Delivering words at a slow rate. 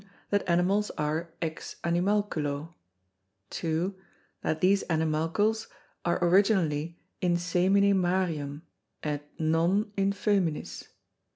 Yes: slow, 100 wpm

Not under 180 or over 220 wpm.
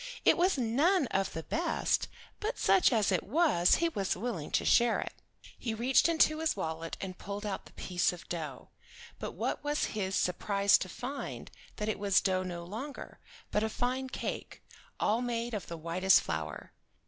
Yes: average, 185 wpm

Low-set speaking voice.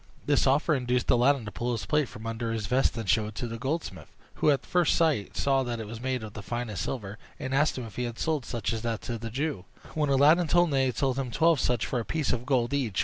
Yes: low, 125 Hz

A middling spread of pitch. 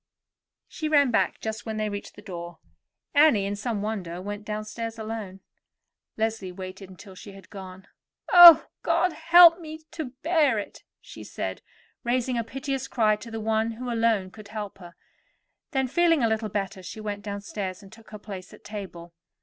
Yes: average, 3.5 semitones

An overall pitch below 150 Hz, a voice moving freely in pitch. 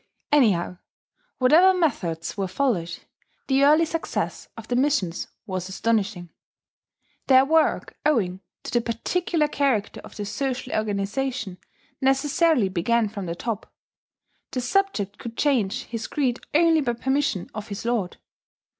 No: high, 235 Hz; wide, 6.0 semitones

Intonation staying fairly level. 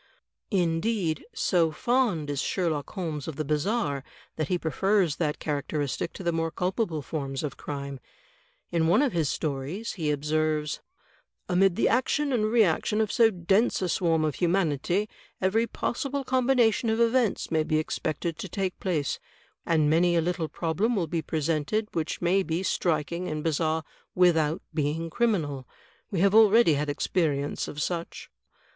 No: average, 4.5 semitones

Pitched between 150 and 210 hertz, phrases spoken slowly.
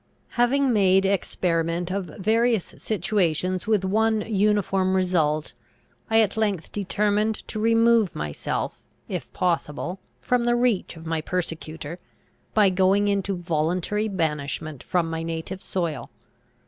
Yes: high, 190 Hz; slow, 120 wpm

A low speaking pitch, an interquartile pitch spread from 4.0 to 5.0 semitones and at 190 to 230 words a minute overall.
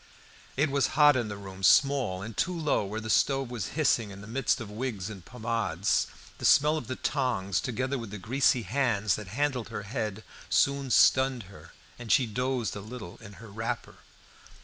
Yes: low, 115 Hz; average, 4.5 semitones; average, 195 wpm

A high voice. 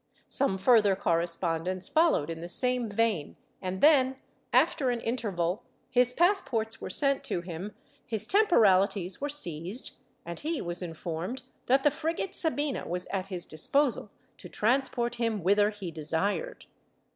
Yes: high, 210 Hz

